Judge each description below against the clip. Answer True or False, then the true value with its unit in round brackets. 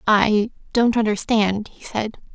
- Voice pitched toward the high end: True (215 Hz)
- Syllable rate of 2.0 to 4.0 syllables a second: True (3.8 syllables/s)